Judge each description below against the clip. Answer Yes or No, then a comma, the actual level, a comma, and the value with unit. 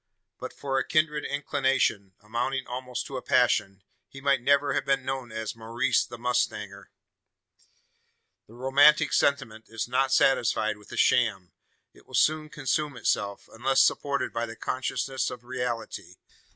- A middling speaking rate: Yes, average, 150 wpm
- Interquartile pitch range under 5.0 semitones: Yes, average, 3.4 semitones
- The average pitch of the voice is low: Yes, low, 125 Hz